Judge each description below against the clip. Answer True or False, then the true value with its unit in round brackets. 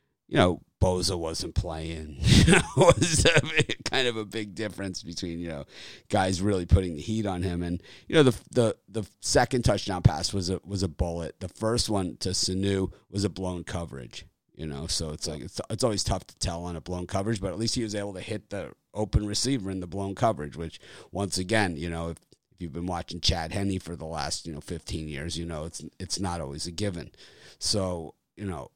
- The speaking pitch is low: True (95 Hz)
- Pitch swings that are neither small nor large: True (3.4 semitones)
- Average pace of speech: False (220 wpm)